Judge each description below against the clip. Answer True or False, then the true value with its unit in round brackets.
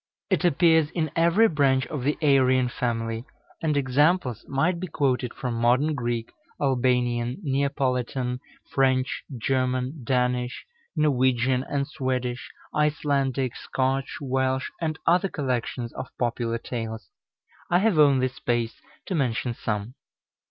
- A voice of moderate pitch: False (130 Hz)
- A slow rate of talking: True (120 wpm)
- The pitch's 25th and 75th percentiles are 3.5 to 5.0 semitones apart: False (2.9 semitones)